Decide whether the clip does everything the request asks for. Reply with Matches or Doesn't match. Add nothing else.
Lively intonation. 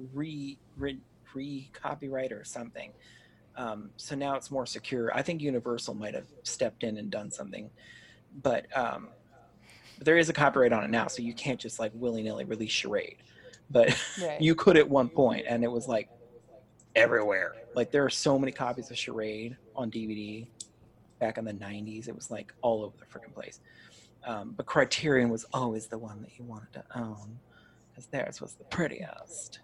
Doesn't match